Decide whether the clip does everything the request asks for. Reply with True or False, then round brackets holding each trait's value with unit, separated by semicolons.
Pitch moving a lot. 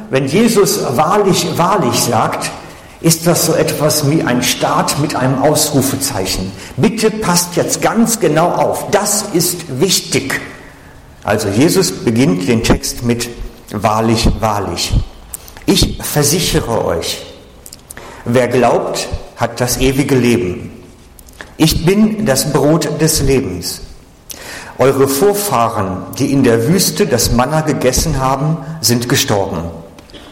True (6.3 semitones)